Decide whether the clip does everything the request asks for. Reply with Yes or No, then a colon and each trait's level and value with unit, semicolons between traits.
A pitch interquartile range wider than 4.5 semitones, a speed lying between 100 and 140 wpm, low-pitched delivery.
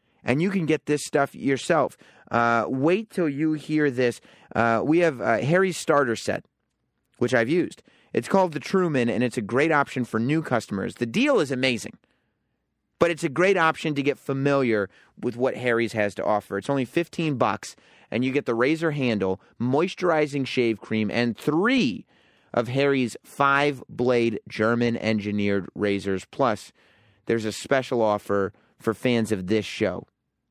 No: average, 5.1 semitones; average, 165 wpm; low, 125 Hz